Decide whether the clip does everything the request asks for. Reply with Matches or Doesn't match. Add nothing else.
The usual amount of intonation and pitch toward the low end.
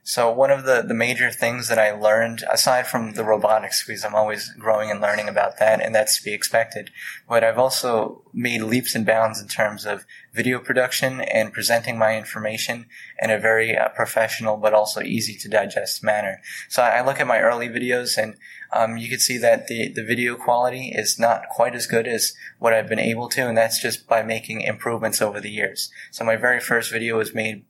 Doesn't match